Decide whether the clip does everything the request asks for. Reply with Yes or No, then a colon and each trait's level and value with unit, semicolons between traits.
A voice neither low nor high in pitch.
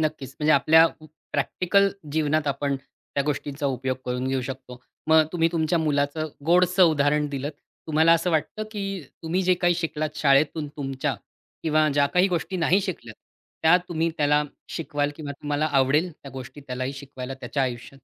Yes: medium, 150 Hz